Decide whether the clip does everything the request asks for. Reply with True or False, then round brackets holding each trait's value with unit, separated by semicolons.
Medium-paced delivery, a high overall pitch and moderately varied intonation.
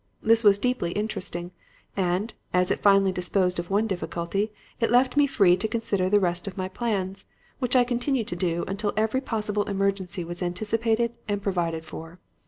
True (180 wpm; 195 Hz; 3.7 semitones)